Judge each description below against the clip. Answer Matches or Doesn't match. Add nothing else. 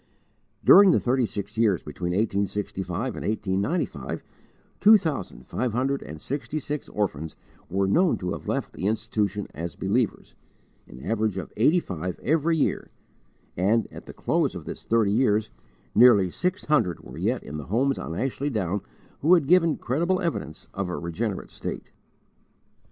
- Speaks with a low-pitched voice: Matches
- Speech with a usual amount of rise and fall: Doesn't match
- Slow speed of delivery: Doesn't match